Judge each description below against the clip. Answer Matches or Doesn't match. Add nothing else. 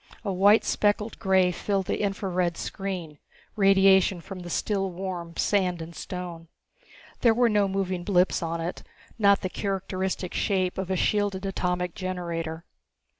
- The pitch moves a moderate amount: Doesn't match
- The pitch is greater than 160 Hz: Matches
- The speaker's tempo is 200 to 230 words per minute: Doesn't match